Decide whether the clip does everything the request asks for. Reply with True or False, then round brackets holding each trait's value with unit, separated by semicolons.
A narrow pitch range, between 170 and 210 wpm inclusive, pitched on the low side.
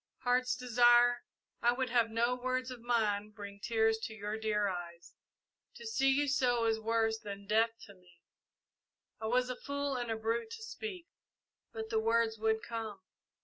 False (2.3 semitones; 175 wpm; 230 Hz)